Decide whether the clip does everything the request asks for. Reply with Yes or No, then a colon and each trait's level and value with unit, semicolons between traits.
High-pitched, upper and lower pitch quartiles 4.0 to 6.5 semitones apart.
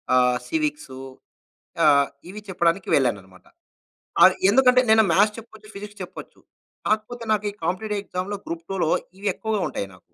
Yes: high, 200 Hz; average, 4.7 semitones